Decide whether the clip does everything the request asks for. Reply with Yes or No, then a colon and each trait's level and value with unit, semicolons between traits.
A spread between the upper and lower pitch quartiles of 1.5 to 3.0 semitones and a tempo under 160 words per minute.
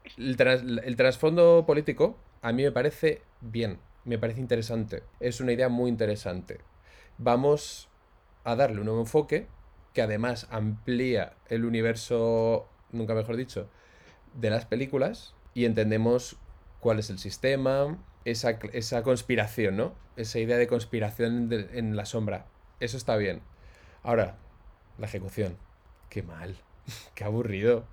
Yes: narrow, 2.5 semitones; average, 130 wpm